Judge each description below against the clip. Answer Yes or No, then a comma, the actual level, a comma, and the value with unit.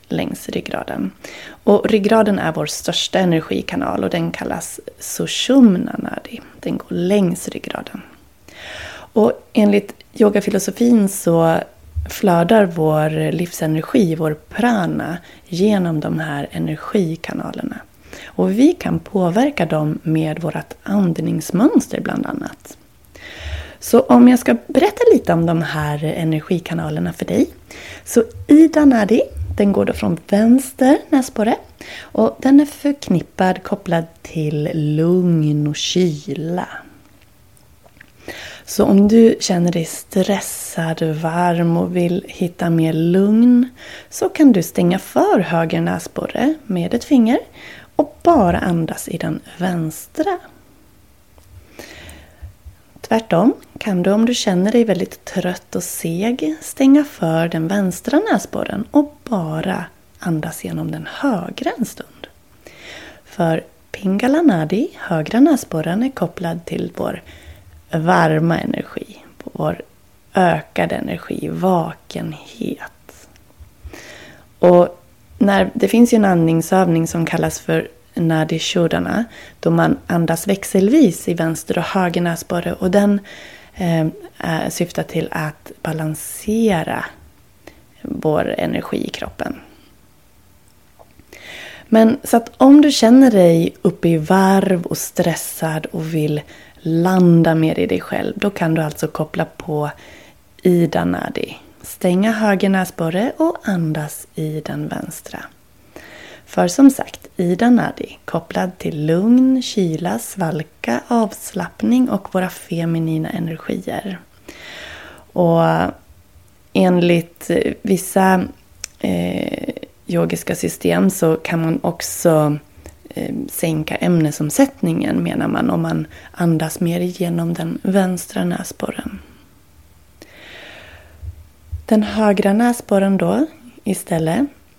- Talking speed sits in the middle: No, slow, 110 wpm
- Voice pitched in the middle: Yes, medium, 175 Hz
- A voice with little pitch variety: No, wide, 5.5 semitones